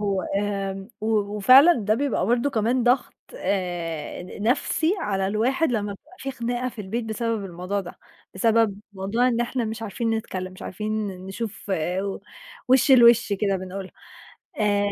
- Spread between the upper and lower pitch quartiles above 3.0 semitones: Yes, average, 3.5 semitones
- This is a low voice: No, high, 215 Hz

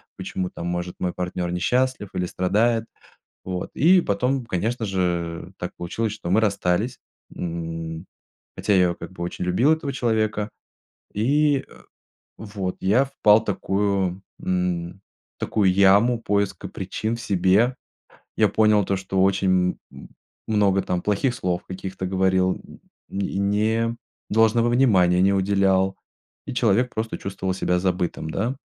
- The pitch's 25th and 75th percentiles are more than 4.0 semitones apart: No, average, 3.5 semitones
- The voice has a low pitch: Yes, very low, 95 Hz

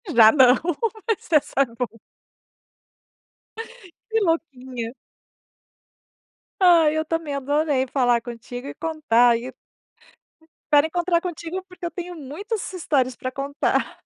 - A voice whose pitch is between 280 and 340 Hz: Yes, very high, 290 Hz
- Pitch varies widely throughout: No, average, 5.0 semitones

